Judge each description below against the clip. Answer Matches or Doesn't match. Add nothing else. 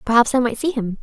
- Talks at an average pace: Doesn't match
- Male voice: Doesn't match